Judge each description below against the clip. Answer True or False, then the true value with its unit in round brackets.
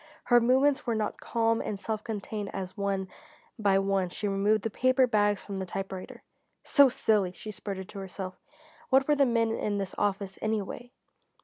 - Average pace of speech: True (180 wpm)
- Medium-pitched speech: False (205 Hz)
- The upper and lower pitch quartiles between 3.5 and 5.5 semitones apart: False (2.8 semitones)